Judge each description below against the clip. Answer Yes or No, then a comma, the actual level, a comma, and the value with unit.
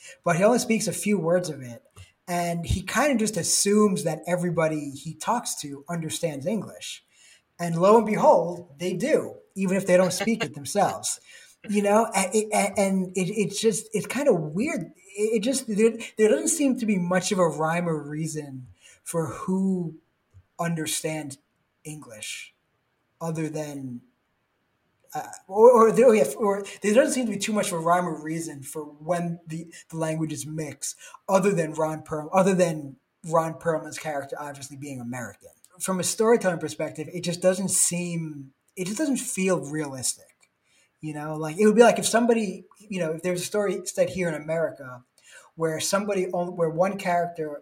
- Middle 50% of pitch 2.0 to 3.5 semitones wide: No, average, 4.6 semitones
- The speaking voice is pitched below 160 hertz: No, medium, 175 Hz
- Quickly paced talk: No, average, 170 wpm